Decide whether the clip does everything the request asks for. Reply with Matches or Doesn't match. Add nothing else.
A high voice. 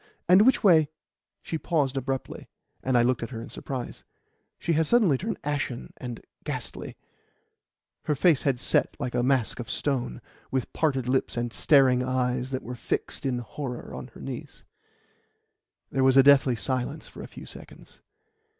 Doesn't match